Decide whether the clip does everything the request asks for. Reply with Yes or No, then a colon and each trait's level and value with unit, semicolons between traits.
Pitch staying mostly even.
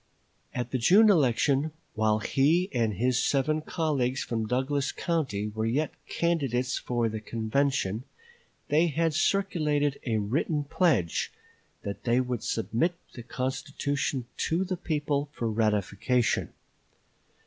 No: average, 5.0 semitones